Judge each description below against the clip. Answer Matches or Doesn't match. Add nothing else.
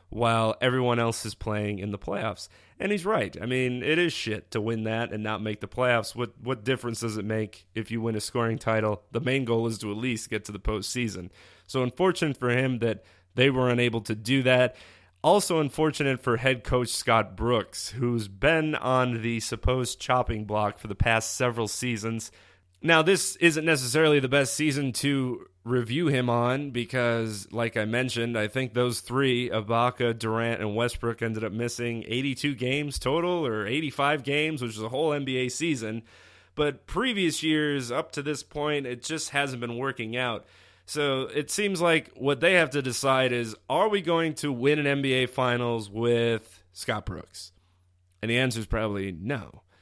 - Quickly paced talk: Doesn't match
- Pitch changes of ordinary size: Matches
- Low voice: Matches